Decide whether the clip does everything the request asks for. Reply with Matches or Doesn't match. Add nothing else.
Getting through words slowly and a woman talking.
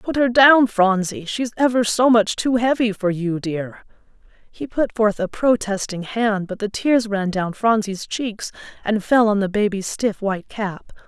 Doesn't match